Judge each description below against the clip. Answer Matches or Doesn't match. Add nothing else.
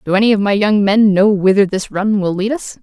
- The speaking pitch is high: Matches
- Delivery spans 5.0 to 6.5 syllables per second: Matches